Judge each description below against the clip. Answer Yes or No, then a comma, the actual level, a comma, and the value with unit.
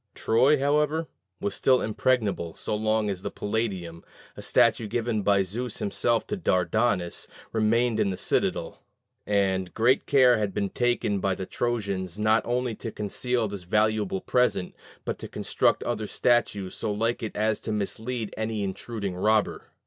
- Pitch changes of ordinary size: Yes, average, 3.3 semitones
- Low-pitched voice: Yes, low, 110 Hz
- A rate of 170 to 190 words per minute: No, average, 155 wpm